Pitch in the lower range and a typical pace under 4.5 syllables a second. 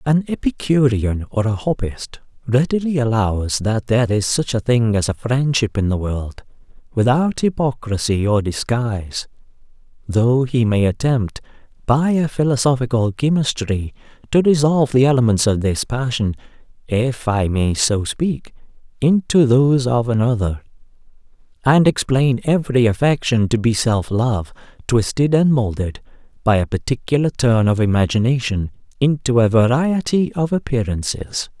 No: low, 120 Hz; 4.6 syllables/s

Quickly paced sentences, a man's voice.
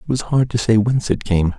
Yes: fast, 305 wpm; male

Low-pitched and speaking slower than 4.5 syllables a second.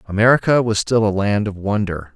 No: low, 105 Hz; 5.6 syllables/s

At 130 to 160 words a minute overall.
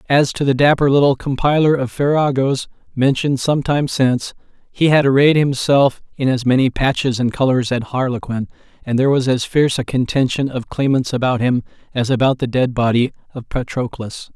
No: average, 175 wpm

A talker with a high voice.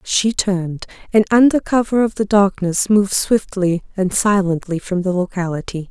Yes: high, 195 Hz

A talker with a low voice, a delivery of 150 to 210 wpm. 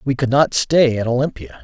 No: low, 130 Hz; fast, 220 wpm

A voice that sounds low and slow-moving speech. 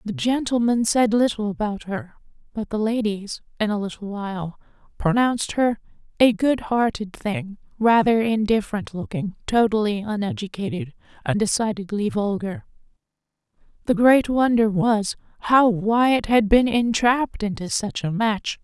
No: high, 215 Hz; slow, 130 wpm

